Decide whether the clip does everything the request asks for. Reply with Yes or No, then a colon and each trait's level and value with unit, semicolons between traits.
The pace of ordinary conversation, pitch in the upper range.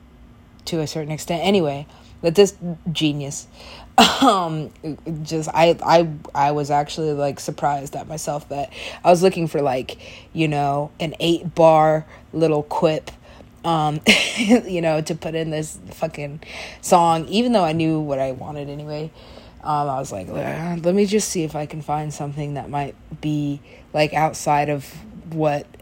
No: average, 160 wpm; medium, 155 Hz